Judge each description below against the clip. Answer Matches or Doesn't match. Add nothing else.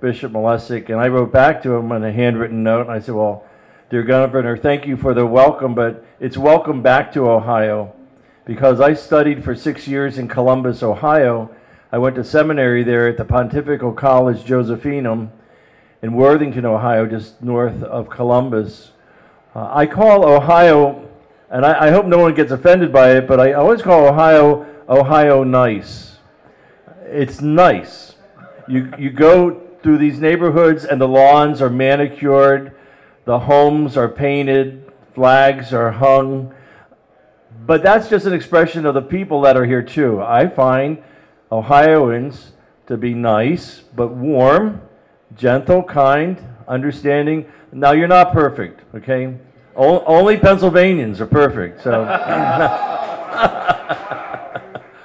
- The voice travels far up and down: Doesn't match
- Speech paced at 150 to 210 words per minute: Doesn't match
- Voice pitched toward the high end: Doesn't match